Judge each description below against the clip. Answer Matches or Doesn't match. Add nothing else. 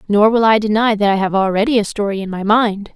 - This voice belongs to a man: Doesn't match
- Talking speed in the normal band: Doesn't match